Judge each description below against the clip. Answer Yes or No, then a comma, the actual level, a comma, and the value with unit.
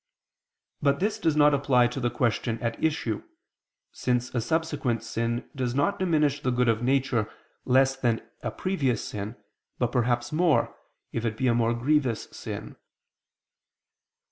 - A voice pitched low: Yes, low, 125 Hz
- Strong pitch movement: No, average, 3.4 semitones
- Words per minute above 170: No, average, 150 wpm